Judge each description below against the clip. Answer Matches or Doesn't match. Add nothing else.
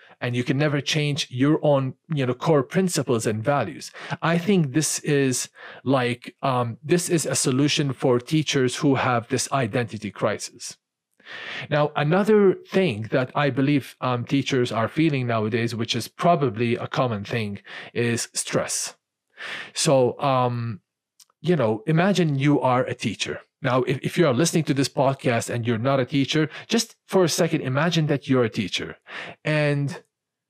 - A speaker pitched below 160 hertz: Matches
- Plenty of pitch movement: Doesn't match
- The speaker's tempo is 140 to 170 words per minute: Matches